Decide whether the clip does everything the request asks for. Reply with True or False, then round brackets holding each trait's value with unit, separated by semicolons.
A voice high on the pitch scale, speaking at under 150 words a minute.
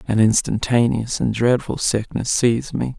False (115 Hz; 140 wpm)